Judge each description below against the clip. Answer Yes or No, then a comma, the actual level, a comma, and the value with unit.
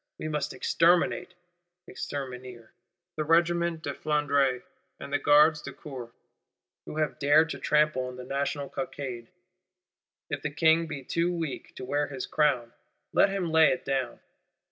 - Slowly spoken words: No, average, 150 wpm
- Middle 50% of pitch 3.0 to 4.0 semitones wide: Yes, average, 3.3 semitones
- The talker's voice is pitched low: No, medium, 145 Hz